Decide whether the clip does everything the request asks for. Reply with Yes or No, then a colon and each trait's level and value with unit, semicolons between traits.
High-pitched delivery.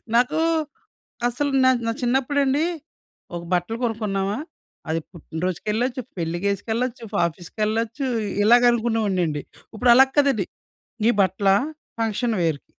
Yes: high, 220 Hz